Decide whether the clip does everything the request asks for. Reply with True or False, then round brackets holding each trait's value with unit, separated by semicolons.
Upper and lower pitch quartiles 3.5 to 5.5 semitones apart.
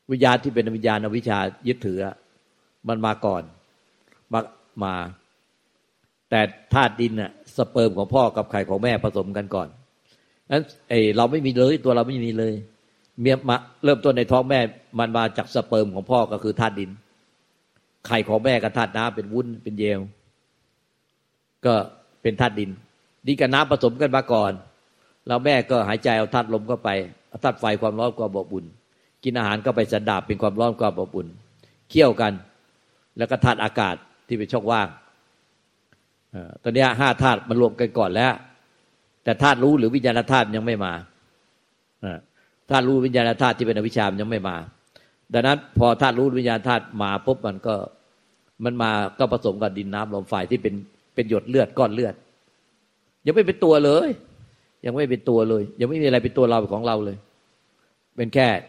False (3.1 semitones)